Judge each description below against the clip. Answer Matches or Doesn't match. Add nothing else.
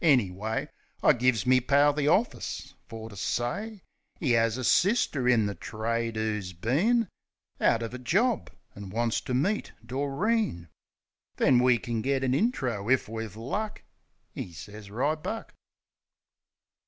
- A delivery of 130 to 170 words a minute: Matches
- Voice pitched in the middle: Doesn't match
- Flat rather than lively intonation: Doesn't match